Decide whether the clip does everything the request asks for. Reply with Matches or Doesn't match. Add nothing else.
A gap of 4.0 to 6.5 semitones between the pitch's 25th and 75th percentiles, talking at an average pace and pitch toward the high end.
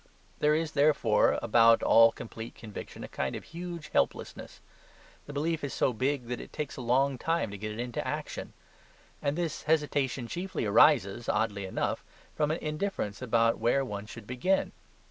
Doesn't match